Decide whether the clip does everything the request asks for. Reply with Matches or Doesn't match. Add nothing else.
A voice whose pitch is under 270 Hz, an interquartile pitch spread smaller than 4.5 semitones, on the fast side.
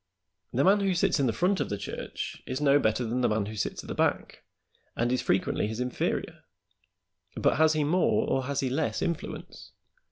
Doesn't match